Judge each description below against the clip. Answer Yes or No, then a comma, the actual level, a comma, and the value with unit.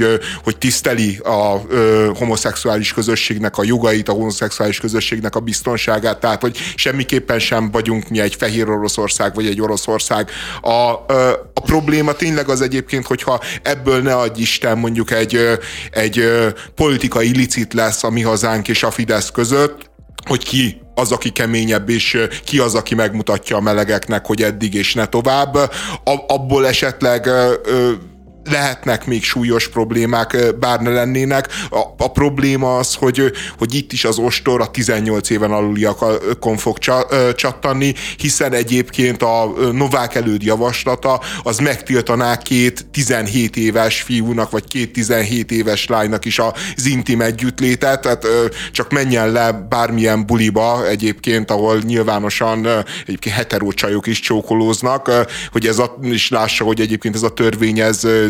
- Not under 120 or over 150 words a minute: Yes, average, 140 wpm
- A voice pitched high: No, low, 115 Hz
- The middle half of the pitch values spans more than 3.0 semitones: No, narrow, 2.4 semitones